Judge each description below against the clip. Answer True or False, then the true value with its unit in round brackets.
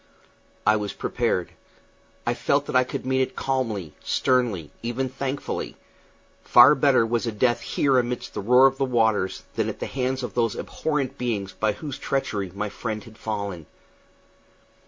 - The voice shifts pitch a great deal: False (3.7 semitones)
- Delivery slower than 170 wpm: True (160 wpm)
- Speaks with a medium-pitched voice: False (120 Hz)